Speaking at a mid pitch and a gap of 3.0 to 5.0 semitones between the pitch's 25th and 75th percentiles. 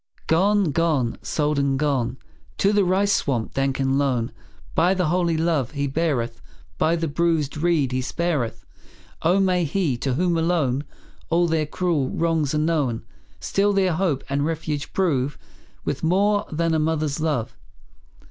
Yes: medium, 155 Hz; average, 3.8 semitones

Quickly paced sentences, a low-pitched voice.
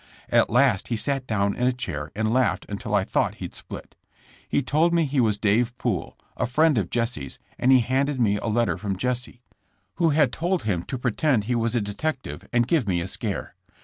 Yes: fast, 215 wpm; low, 120 Hz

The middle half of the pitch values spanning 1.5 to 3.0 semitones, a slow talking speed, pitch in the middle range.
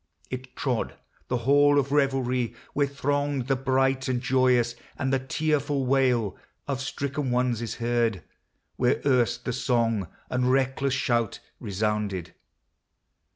No: narrow, 2.4 semitones; slow, 130 wpm; low, 130 Hz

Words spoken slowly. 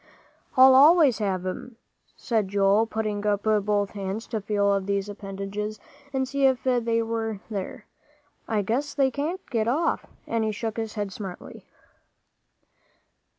No: average, 150 wpm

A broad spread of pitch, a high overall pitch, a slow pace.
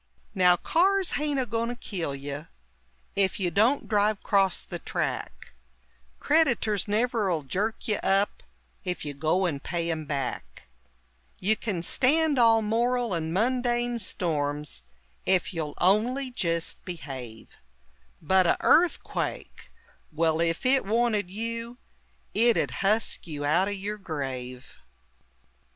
Yes: wide, 6.4 semitones; high, 195 Hz; slow, 130 wpm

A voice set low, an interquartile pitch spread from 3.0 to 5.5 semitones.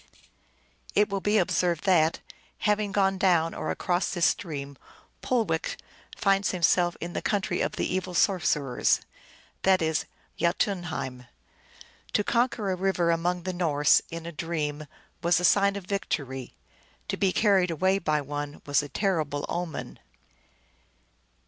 No: medium, 175 Hz; average, 3.6 semitones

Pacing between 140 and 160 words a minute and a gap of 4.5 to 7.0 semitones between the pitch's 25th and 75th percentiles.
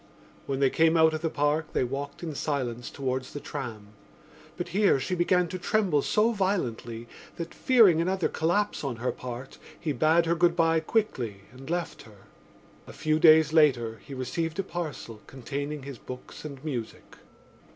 No: average, 170 wpm; average, 4.8 semitones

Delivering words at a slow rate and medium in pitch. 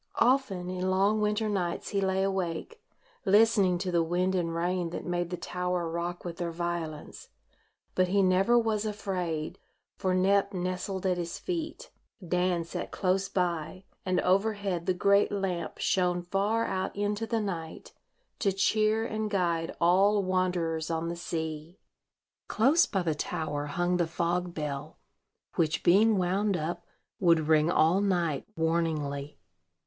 No: average, 150 wpm; medium, 180 Hz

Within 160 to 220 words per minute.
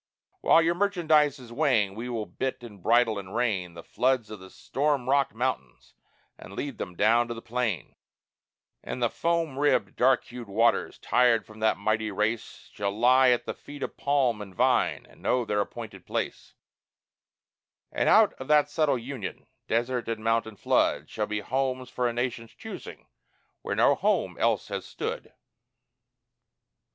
Yes: average, 165 wpm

